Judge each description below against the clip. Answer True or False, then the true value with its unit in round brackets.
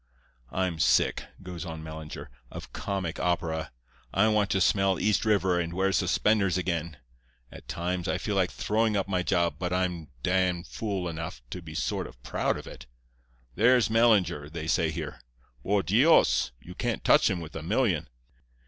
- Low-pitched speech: True (90 Hz)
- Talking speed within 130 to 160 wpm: False (170 wpm)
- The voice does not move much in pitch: False (3.1 semitones)